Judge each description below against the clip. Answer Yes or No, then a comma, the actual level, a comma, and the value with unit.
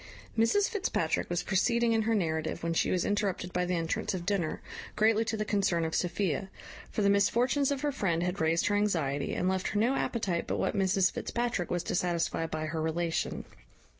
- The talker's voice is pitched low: No, high, 190 Hz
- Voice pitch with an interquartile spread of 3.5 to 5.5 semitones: Yes, average, 4.4 semitones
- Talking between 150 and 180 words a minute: No, average, 200 wpm